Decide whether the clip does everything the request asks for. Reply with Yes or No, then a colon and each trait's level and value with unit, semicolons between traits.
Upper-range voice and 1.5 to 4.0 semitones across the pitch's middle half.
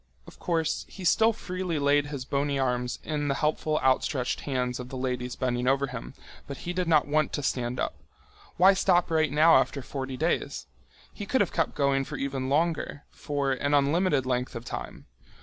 No: medium, 140 Hz; average, 3.4 semitones